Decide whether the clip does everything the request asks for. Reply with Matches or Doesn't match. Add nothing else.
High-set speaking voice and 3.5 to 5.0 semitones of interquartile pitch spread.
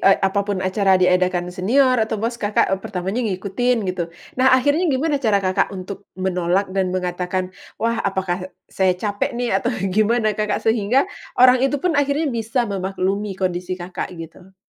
Matches